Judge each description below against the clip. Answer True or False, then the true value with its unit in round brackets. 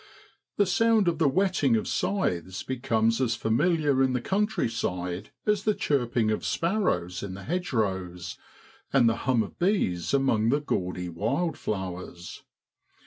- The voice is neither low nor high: False (120 Hz)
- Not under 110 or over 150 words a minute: True (140 wpm)